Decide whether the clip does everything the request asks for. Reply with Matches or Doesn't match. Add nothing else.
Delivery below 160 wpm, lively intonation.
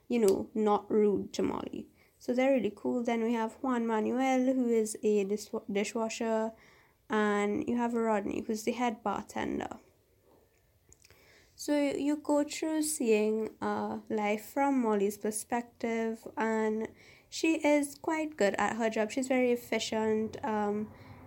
Doesn't match